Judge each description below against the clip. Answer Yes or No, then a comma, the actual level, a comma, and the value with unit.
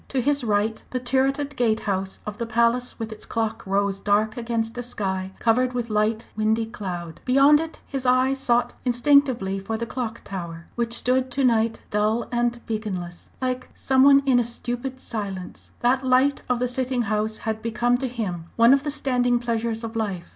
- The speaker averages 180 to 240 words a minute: Yes, average, 190 wpm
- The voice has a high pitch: Yes, high, 235 Hz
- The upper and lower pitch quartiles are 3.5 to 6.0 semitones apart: No, average, 2.8 semitones